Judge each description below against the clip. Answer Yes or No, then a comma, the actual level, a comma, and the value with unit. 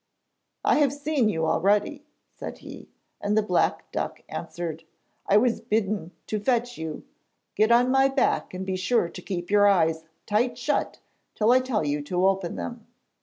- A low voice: No, high, 205 Hz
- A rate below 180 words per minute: Yes, average, 170 wpm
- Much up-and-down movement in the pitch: Yes, wide, 5.7 semitones